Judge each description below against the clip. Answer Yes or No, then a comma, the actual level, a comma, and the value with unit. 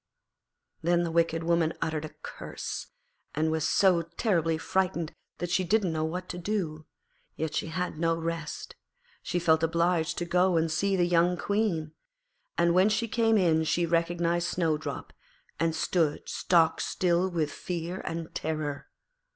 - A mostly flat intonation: Yes, narrow, 1.9 semitones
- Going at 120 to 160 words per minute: Yes, average, 155 wpm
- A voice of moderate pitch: Yes, medium, 170 Hz